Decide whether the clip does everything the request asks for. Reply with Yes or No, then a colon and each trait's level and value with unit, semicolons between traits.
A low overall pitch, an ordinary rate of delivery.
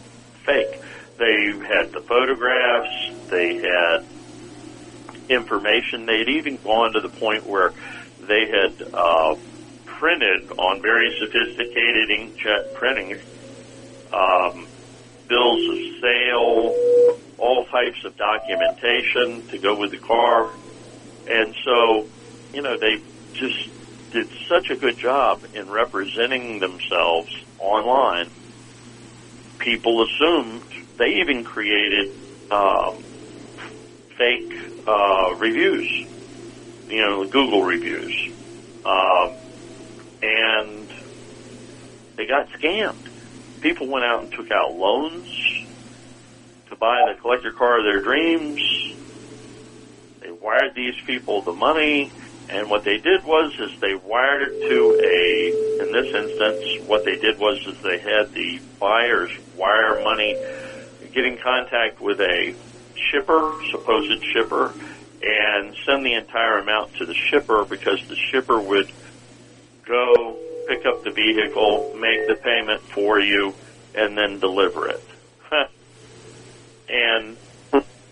No: low, 125 Hz; slow, 115 wpm